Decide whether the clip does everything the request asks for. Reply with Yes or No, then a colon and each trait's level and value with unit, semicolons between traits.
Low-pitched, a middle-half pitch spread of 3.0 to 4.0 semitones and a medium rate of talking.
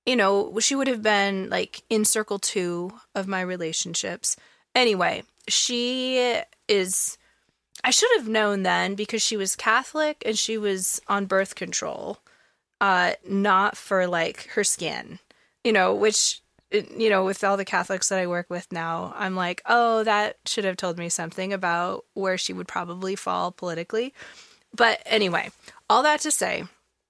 No: high, 200 Hz; average, 3.4 semitones; average, 160 wpm